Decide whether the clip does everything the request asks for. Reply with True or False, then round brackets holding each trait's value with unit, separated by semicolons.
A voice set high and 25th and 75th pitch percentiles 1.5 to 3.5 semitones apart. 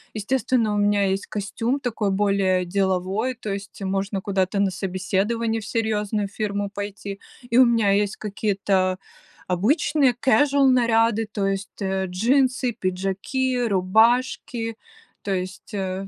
True (205 Hz; 3.1 semitones)